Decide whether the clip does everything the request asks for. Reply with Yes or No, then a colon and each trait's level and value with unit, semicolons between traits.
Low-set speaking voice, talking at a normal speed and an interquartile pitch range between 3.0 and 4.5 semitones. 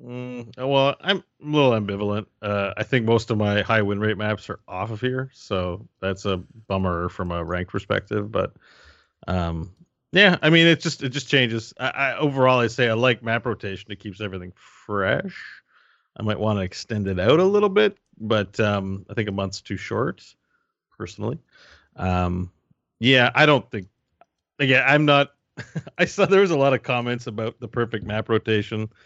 No: low, 110 Hz; average, 190 wpm; average, 4.9 semitones